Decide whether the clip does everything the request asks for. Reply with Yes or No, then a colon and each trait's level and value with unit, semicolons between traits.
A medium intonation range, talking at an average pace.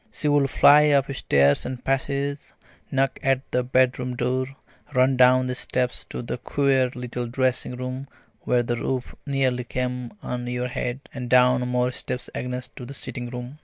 No: narrow, 1.2 semitones; average, 170 wpm